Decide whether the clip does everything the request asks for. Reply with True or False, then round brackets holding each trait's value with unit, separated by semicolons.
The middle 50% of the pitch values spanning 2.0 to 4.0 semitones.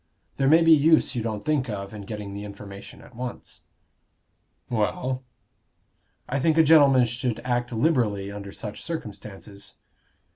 False (5.1 semitones)